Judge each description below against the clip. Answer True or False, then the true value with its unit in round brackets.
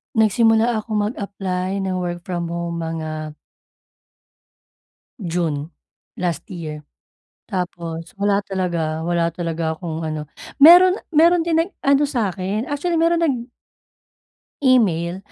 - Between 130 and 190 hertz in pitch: True (185 Hz)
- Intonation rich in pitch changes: True (5.8 semitones)